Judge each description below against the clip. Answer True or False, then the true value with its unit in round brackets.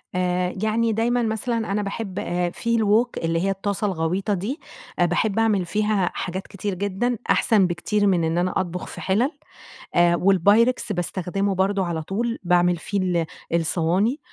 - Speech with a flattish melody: False (3.5 semitones)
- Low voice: False (195 Hz)